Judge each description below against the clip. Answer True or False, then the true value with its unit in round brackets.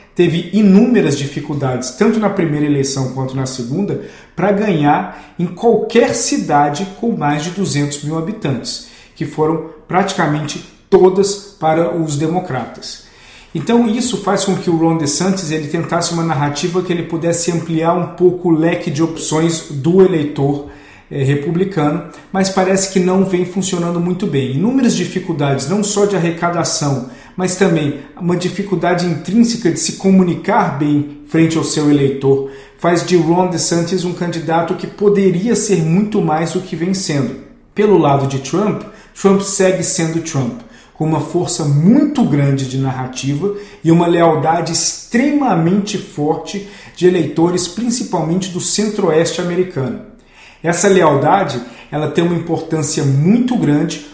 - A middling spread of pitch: True (3.9 semitones)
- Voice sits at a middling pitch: True (170 Hz)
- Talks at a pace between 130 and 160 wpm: True (145 wpm)